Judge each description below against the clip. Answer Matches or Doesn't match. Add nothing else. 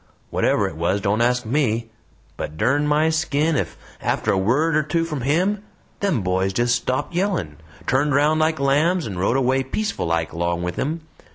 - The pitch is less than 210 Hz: Matches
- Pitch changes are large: Matches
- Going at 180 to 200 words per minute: Matches